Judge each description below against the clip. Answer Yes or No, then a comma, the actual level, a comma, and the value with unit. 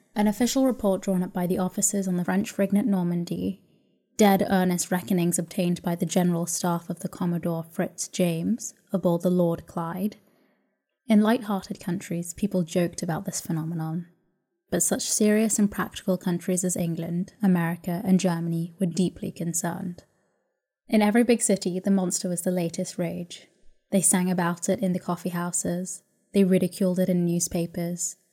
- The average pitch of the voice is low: No, medium, 180 Hz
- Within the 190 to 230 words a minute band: No, average, 160 wpm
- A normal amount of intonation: No, narrow, 2.0 semitones